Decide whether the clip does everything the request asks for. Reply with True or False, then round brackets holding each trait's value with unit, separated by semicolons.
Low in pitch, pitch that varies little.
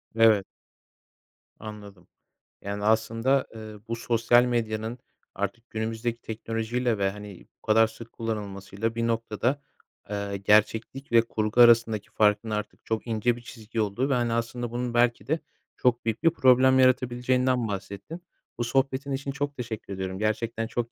True (115 Hz; 2.2 semitones)